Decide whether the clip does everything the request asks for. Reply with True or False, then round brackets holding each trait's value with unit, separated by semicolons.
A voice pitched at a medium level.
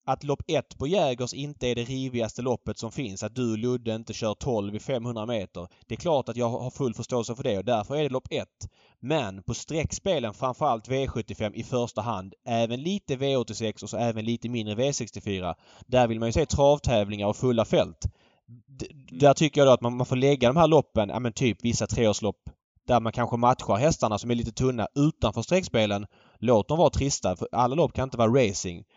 False (120 Hz)